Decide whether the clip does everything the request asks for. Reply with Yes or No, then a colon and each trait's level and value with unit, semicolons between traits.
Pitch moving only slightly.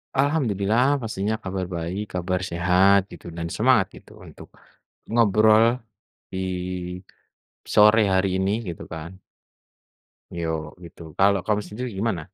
No: average, 3.3 semitones